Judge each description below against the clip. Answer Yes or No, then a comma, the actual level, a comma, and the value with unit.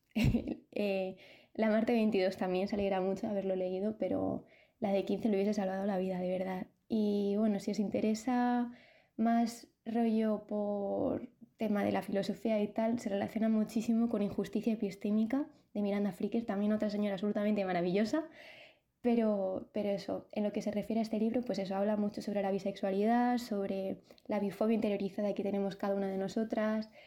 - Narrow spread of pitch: Yes, narrow, 2.2 semitones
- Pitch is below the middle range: No, high, 210 Hz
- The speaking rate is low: No, average, 170 wpm